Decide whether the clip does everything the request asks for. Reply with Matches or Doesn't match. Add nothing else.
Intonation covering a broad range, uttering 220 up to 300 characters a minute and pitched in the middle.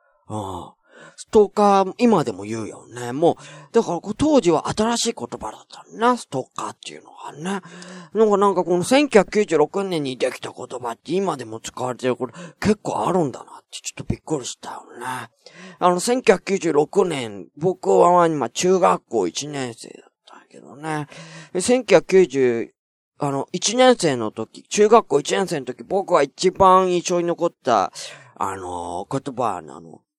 Matches